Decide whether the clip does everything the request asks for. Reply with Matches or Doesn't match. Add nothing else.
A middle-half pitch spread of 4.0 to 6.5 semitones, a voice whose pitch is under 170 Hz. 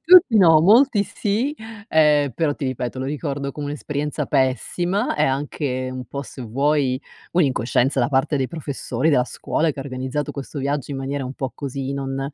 Doesn't match